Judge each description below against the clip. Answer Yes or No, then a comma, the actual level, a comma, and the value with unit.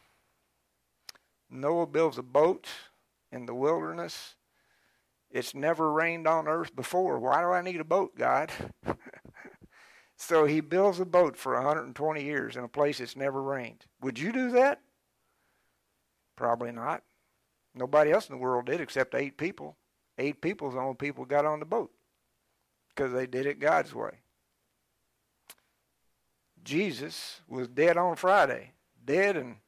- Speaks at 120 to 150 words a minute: Yes, average, 140 wpm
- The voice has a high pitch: No, medium, 145 Hz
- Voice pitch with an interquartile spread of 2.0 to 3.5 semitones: No, average, 4.5 semitones